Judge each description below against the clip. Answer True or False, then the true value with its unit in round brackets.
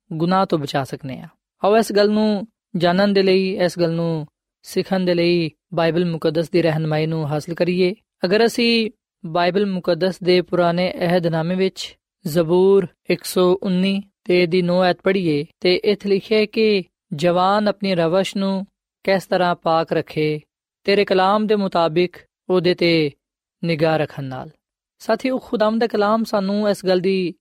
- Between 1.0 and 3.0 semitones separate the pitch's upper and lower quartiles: True (2.7 semitones)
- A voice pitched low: False (180 Hz)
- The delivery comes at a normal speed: True (155 wpm)